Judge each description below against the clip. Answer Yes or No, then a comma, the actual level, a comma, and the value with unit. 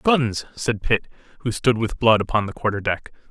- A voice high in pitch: No, low, 115 Hz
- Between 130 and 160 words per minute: No, average, 200 wpm